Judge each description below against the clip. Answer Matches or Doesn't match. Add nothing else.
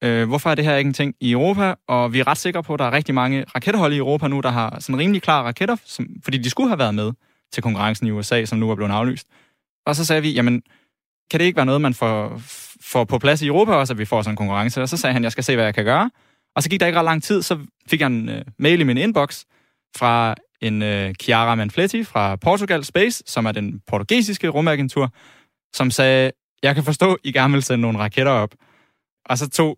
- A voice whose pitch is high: Doesn't match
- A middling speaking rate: Doesn't match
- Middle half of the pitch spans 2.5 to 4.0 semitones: Doesn't match